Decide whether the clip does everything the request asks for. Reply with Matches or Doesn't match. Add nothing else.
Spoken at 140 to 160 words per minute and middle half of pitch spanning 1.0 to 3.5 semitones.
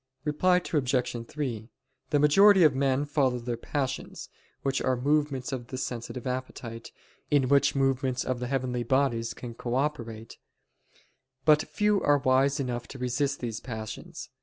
Matches